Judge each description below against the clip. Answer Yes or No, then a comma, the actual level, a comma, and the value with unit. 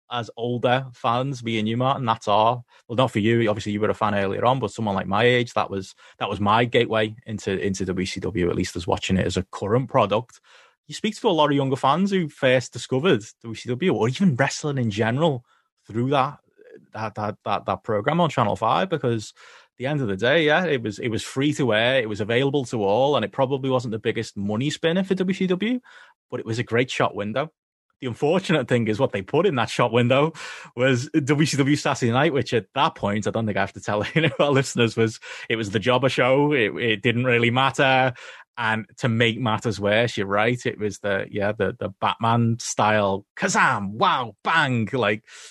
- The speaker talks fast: Yes, fast, 220 wpm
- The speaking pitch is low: Yes, low, 120 Hz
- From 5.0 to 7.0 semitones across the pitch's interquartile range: No, average, 4.0 semitones